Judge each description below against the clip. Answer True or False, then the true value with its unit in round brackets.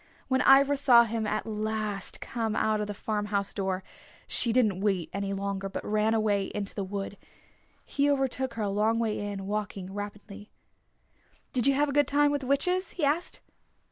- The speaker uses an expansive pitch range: False (4.6 semitones)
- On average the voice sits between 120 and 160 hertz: False (215 Hz)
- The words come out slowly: False (185 wpm)